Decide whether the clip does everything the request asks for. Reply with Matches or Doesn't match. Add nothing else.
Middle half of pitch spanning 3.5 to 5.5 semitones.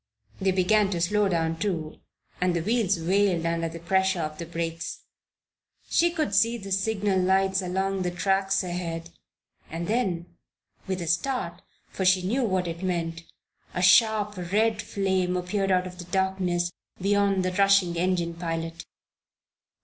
Doesn't match